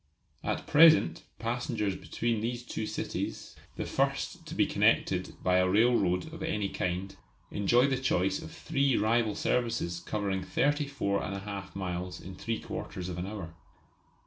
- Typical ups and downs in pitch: Yes, average, 4.5 semitones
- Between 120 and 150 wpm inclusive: Yes, average, 145 wpm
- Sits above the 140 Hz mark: No, low, 105 Hz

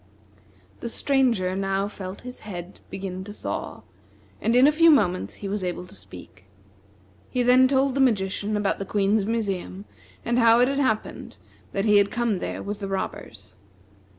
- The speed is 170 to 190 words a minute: Yes, average, 175 wpm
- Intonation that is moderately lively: Yes, average, 4.2 semitones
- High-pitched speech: Yes, high, 205 Hz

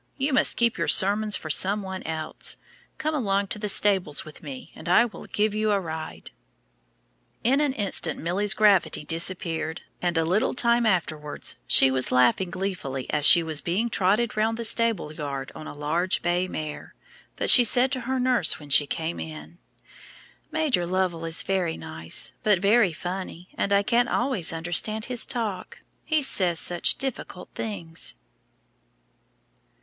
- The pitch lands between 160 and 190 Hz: Yes, medium, 185 Hz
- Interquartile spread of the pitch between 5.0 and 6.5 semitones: Yes, average, 5.3 semitones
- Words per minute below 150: No, average, 165 wpm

